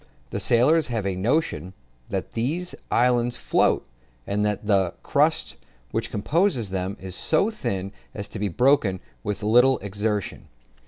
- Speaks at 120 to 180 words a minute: Yes, average, 145 wpm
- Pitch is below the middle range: Yes, low, 110 Hz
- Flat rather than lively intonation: No, average, 4.3 semitones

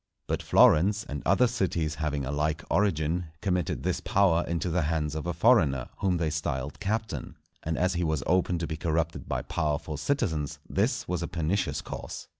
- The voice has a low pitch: Yes, very low, 80 Hz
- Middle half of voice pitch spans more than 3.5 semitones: No, average, 3.0 semitones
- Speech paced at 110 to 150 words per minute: No, average, 185 wpm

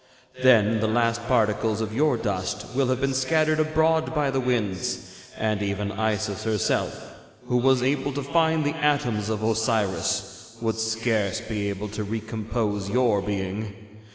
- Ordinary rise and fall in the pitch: Yes, average, 3.8 semitones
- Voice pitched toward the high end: No, low, 110 Hz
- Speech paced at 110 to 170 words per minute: Yes, average, 155 wpm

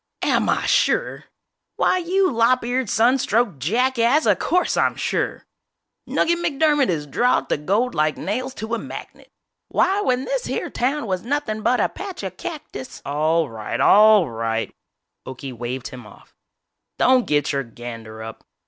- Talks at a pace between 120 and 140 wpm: No, average, 165 wpm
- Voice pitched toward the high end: Yes, high, 220 Hz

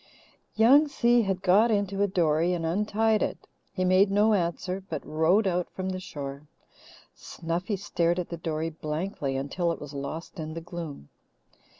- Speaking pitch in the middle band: Yes, medium, 180 Hz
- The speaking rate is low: No, average, 170 wpm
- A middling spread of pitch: Yes, average, 3.8 semitones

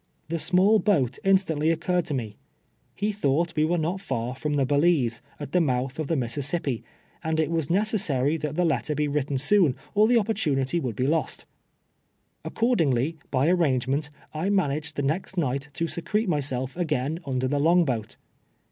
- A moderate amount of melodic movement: Yes, average, 4.5 semitones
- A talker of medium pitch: Yes, medium, 150 Hz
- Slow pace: No, average, 175 wpm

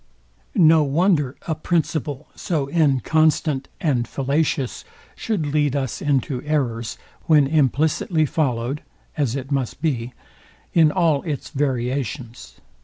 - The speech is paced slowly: Yes, slow, 110 wpm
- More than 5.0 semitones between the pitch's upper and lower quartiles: No, average, 3.1 semitones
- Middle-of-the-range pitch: Yes, medium, 145 Hz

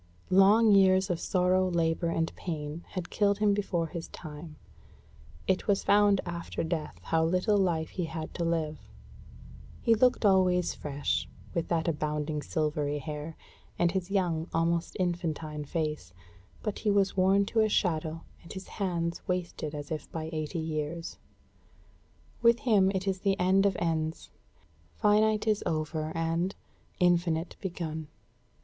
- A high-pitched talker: No, medium, 170 Hz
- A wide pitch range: No, average, 3.3 semitones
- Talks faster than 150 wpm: No, average, 145 wpm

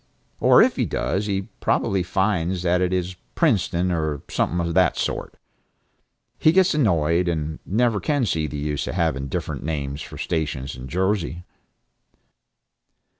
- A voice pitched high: No, very low, 85 Hz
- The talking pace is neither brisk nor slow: Yes, average, 150 wpm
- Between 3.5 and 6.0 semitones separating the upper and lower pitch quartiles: Yes, average, 3.8 semitones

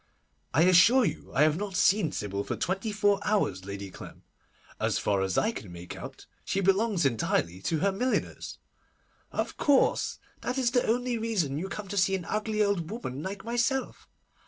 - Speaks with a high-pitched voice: Yes, high, 195 Hz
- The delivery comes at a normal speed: Yes, average, 180 wpm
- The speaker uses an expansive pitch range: Yes, wide, 7.3 semitones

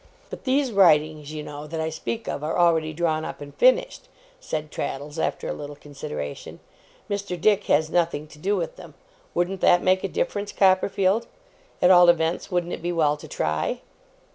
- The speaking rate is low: No, average, 185 wpm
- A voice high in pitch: No, medium, 170 Hz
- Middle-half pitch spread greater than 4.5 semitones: No, average, 4.2 semitones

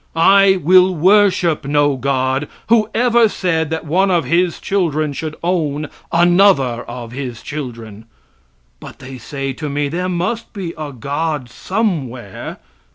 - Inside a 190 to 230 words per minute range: No, average, 140 wpm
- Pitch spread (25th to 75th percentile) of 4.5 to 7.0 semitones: Yes, average, 5.0 semitones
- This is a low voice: No, medium, 155 Hz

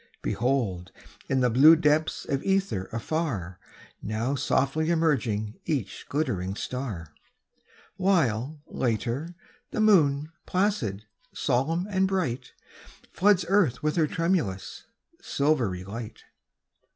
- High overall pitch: No, medium, 140 Hz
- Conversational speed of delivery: No, slow, 105 wpm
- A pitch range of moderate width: No, wide, 6.9 semitones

